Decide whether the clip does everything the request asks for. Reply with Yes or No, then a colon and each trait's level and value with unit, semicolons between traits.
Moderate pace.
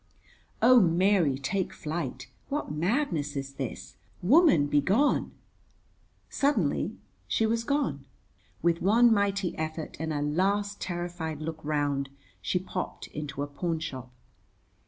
No: slow, 120 wpm